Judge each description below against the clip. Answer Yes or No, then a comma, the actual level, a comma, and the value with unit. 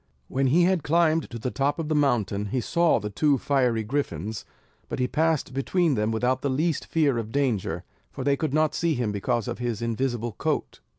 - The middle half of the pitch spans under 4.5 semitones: No, average, 5.1 semitones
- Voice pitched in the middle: No, low, 130 Hz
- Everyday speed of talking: No, fast, 210 wpm